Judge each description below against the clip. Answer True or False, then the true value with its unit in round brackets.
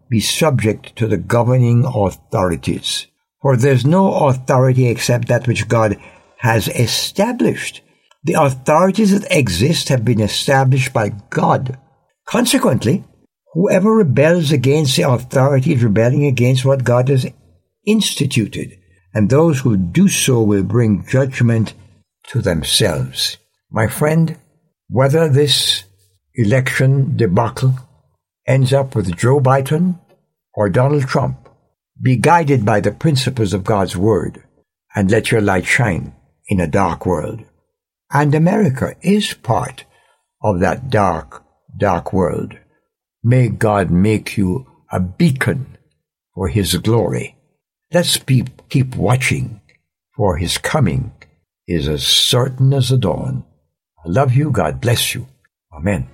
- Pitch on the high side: False (130 Hz)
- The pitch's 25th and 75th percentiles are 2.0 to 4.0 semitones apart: False (4.6 semitones)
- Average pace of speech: False (125 wpm)